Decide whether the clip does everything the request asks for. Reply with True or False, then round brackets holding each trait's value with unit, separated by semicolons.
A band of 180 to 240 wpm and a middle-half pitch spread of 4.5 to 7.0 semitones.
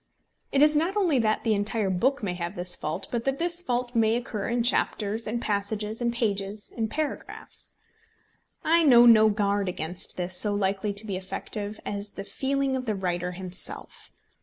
False (185 wpm; 3.7 semitones)